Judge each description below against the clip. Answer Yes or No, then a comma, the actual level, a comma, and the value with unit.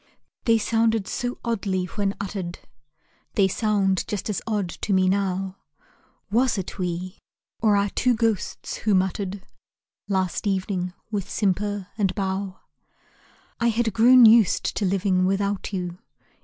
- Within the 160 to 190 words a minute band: No, slow, 135 wpm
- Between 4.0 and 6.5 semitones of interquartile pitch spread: No, narrow, 2.5 semitones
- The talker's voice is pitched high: Yes, high, 200 Hz